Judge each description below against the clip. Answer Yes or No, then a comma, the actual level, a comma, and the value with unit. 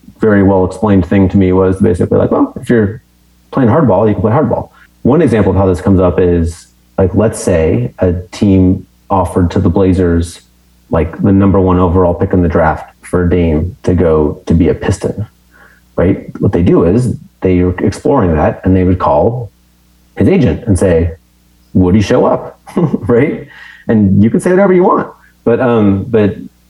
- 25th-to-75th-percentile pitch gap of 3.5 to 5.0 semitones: No, average, 2.7 semitones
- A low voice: Yes, very low, 90 Hz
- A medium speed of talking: Yes, average, 185 wpm